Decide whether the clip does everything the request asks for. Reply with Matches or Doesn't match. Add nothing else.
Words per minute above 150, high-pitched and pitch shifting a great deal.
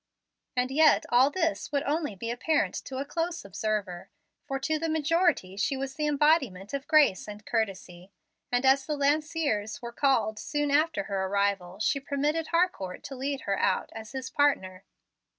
Matches